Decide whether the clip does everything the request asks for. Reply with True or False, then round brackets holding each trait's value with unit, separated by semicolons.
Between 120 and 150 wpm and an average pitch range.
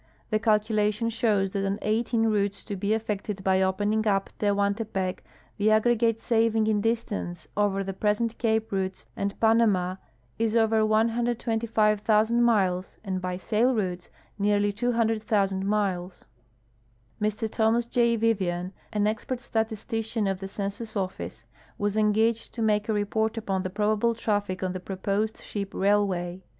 False (145 wpm; 2.3 semitones)